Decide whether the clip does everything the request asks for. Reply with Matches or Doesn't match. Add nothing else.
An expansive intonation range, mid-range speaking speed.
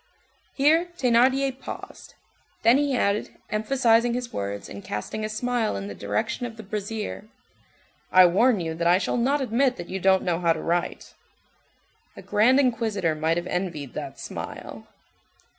Matches